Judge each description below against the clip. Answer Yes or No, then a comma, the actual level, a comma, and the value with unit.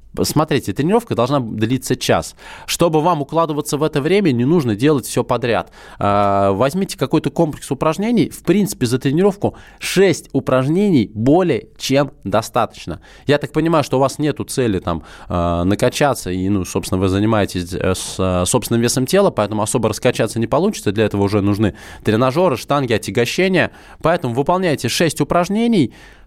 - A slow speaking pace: No, average, 145 wpm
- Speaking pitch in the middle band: No, low, 130 Hz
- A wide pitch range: Yes, wide, 6.9 semitones